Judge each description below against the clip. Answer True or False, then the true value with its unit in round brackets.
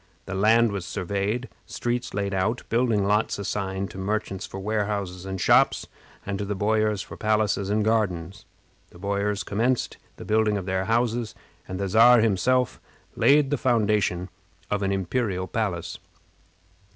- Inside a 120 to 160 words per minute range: True (150 wpm)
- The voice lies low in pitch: True (105 Hz)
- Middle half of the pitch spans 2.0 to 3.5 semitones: True (2.6 semitones)